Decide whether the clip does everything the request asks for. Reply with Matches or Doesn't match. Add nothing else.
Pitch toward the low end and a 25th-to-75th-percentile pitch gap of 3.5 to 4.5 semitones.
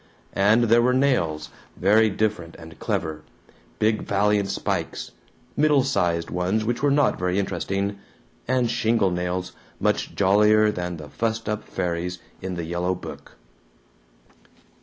Matches